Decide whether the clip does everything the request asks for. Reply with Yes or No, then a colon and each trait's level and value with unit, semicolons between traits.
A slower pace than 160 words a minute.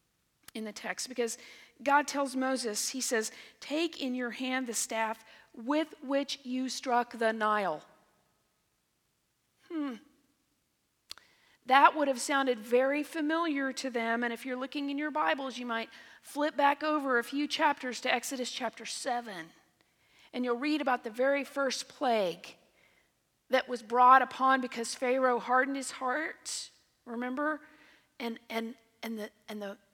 Yes: average, 145 wpm